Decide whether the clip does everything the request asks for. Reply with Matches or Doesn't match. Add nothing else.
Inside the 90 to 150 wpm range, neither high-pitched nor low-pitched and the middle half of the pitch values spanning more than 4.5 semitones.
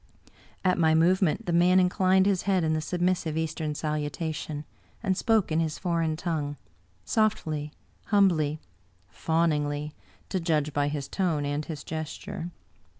Doesn't match